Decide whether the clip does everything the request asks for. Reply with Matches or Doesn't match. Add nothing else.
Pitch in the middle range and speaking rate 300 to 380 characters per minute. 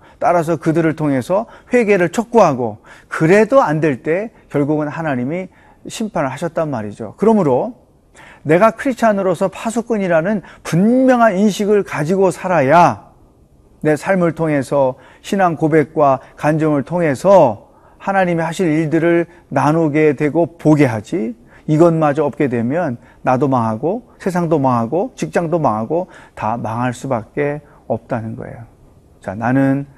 Doesn't match